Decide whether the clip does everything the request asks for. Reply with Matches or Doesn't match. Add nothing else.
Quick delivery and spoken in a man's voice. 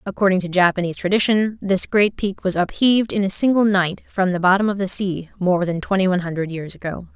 Doesn't match